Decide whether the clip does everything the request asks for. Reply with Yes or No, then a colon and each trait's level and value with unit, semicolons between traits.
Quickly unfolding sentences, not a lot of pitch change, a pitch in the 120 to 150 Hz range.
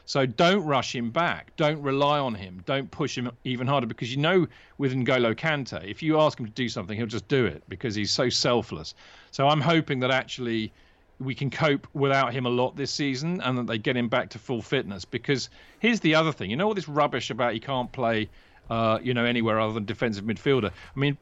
No: fast, 230 wpm; average, 3.8 semitones; low, 130 Hz